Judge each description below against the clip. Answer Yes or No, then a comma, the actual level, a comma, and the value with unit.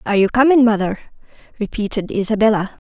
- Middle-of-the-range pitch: No, high, 215 Hz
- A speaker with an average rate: No, slow, 125 wpm